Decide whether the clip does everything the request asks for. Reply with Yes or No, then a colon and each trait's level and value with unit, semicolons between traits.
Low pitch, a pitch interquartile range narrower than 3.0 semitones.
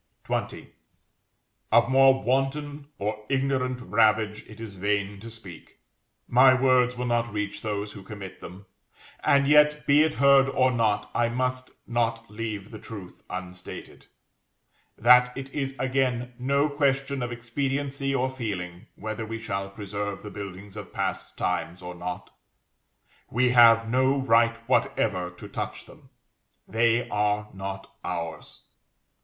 No: low, 115 Hz; average, 4.3 semitones